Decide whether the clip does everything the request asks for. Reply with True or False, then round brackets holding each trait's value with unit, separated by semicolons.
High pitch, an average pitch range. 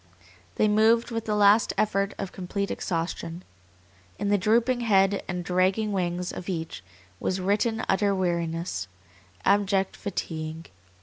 True (195 Hz; 3.0 semitones)